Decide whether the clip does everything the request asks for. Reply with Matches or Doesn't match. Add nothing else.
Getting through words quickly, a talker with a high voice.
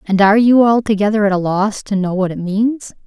Matches